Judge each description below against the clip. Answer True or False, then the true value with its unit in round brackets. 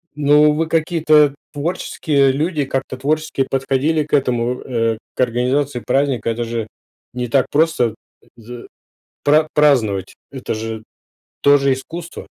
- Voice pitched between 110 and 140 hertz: True (135 Hz)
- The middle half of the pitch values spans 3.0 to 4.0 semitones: True (3.6 semitones)